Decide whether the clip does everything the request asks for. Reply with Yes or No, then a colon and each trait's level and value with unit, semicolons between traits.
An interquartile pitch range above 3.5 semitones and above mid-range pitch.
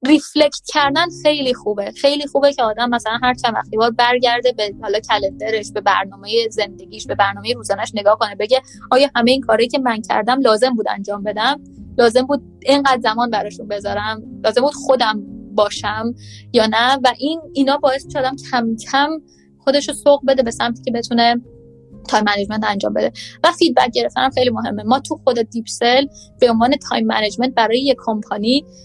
Yes: average, 3.9 semitones; high, 240 Hz